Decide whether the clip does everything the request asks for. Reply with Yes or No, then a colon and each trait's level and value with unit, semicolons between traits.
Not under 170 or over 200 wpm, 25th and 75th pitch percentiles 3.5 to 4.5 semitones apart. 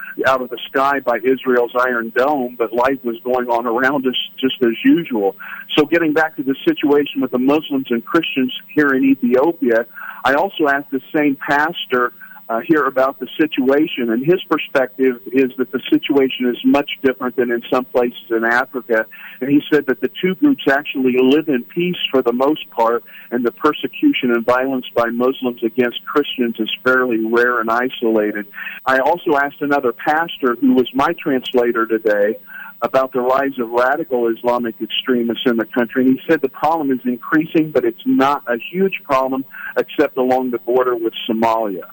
No: average, 180 wpm; average, 3.1 semitones